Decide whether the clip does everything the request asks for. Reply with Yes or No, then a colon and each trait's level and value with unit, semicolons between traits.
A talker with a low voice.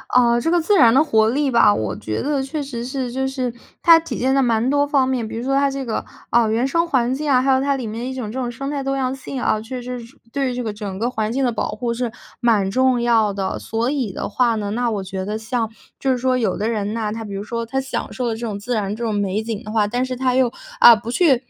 No: high, 240 Hz